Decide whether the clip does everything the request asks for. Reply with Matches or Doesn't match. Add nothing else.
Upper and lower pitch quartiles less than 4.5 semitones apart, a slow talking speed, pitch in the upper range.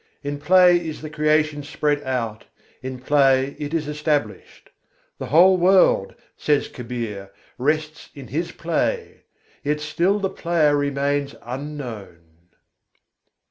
Doesn't match